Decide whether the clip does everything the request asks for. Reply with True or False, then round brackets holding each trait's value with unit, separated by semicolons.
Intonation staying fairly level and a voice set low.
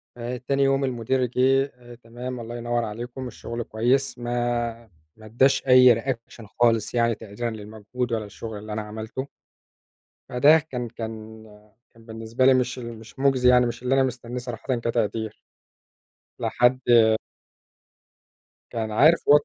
True (2.2 semitones; 120 Hz)